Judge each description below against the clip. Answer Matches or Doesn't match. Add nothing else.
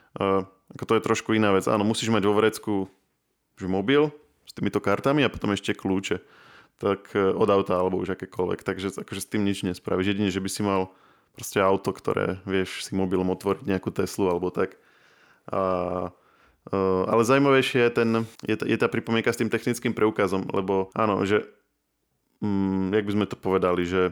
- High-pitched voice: Doesn't match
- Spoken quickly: Matches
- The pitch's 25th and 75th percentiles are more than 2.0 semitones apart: Matches